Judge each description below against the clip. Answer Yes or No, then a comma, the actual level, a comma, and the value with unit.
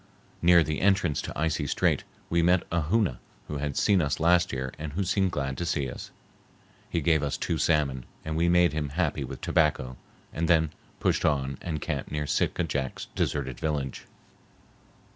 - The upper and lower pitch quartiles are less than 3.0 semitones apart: No, average, 3.3 semitones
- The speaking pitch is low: Yes, very low, 75 Hz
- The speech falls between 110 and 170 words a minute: No, average, 180 wpm